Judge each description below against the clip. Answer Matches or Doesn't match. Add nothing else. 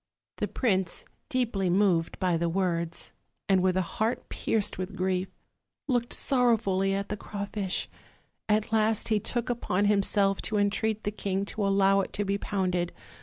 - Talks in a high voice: Matches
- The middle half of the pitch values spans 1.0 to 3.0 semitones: Matches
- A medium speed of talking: Matches